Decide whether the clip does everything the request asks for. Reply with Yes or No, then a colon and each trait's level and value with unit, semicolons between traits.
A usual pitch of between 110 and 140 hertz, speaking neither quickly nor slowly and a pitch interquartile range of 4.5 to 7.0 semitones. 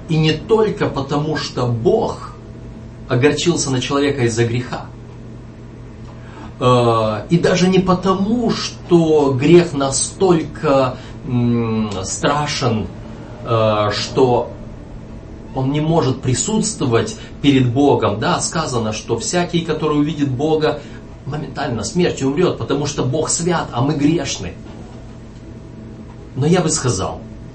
No: low, 130 Hz; slow, 100 wpm; average, 5.1 semitones